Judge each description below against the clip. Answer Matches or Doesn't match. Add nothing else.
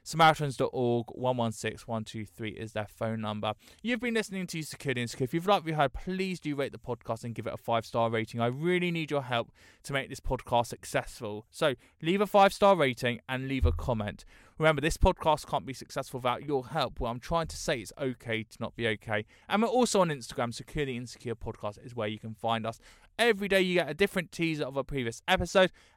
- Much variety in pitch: Matches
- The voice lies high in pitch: Doesn't match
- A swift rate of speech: Matches